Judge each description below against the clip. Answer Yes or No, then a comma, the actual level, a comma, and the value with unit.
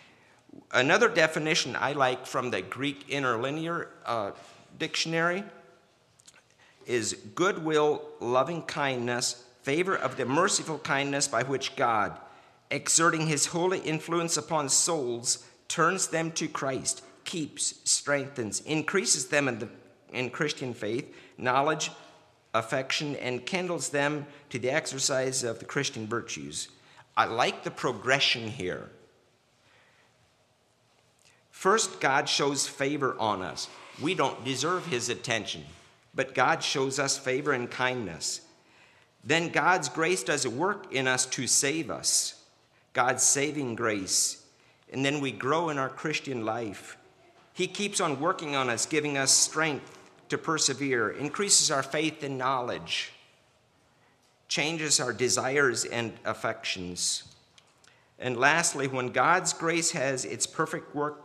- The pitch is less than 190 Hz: Yes, medium, 140 Hz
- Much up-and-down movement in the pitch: No, average, 4.1 semitones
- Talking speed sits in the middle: No, slow, 125 wpm